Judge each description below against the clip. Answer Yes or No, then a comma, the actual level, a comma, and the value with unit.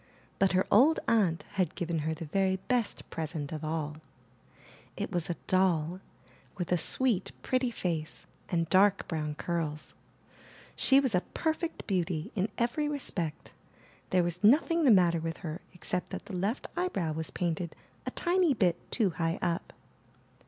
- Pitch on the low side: No, medium, 180 Hz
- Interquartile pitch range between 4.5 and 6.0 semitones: Yes, average, 5.2 semitones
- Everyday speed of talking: Yes, average, 160 wpm